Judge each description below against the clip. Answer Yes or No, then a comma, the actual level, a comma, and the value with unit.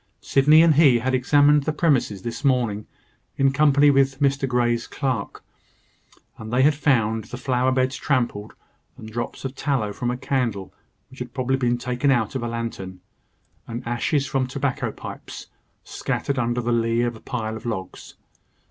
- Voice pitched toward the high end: No, low, 125 Hz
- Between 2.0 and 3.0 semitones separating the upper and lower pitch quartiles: Yes, average, 2.7 semitones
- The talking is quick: No, average, 170 wpm